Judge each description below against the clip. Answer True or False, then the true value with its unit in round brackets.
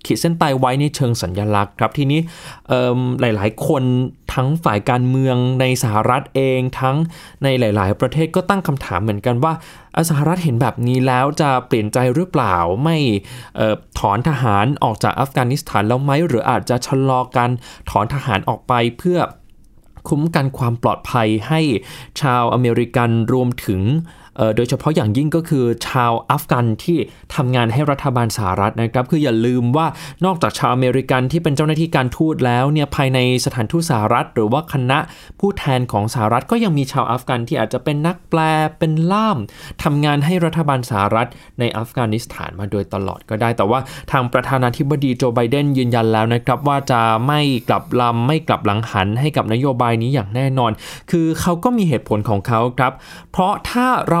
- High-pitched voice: False (130 Hz)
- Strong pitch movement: False (4.4 semitones)